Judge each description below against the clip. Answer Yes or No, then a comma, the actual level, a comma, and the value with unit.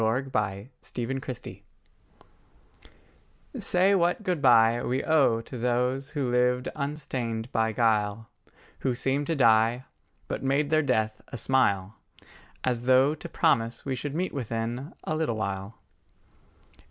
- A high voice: No, low, 125 Hz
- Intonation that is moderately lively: Yes, average, 3.7 semitones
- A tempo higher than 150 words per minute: No, slow, 135 wpm